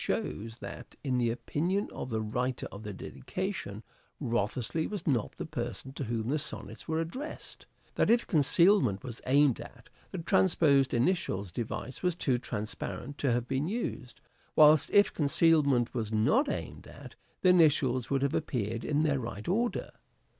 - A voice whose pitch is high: No, low, 135 Hz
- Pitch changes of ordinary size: No, wide, 5.7 semitones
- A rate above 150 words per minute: Yes, average, 160 wpm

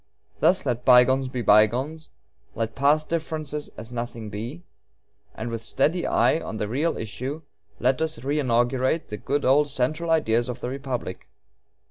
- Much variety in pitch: No, average, 4.3 semitones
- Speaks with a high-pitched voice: No, low, 130 Hz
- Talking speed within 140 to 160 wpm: Yes, average, 150 wpm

